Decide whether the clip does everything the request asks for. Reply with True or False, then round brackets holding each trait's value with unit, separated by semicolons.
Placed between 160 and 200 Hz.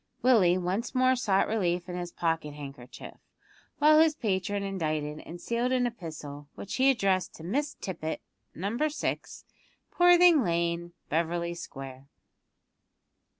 True (185 Hz)